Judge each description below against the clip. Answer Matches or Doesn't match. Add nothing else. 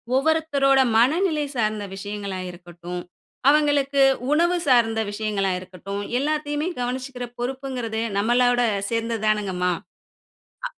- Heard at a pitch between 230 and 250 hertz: Matches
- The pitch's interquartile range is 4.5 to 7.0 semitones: Matches